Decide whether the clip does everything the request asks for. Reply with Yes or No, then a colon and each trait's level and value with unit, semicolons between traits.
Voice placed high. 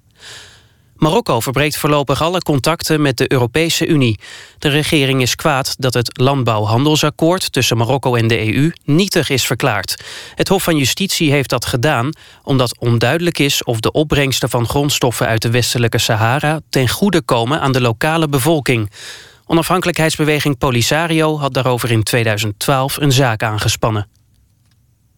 No: low, 135 Hz